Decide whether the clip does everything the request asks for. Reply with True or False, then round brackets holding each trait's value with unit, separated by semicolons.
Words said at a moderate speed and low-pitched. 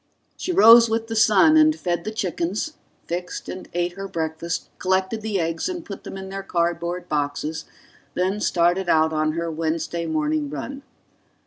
False (170 wpm; 175 Hz)